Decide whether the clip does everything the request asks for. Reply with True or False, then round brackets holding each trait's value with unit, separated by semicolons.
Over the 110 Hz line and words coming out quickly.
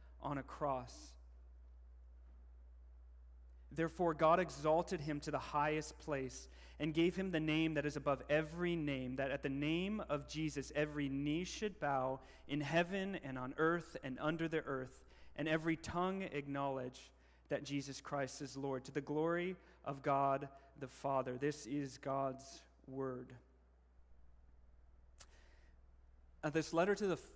False (140 Hz; 145 wpm)